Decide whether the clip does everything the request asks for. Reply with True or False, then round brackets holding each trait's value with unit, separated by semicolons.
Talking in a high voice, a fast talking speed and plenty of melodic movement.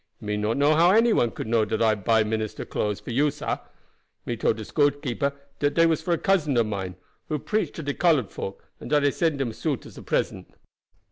False (140 Hz; 225 wpm; 5.8 semitones)